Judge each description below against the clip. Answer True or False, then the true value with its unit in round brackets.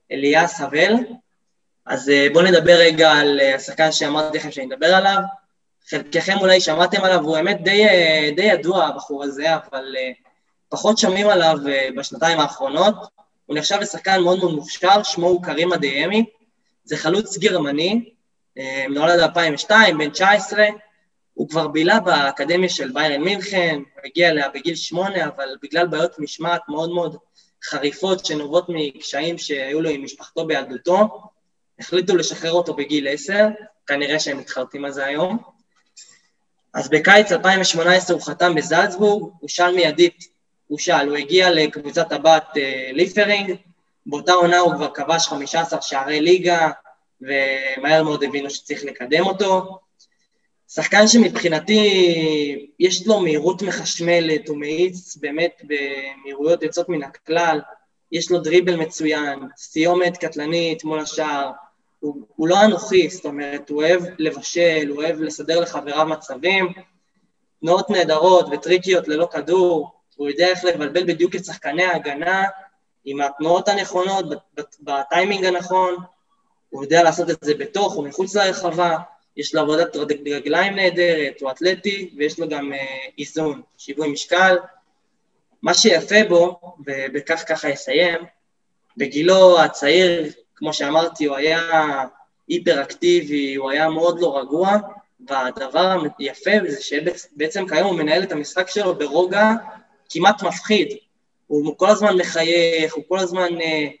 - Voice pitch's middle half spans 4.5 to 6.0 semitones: False (3.8 semitones)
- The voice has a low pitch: False (165 Hz)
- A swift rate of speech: False (130 wpm)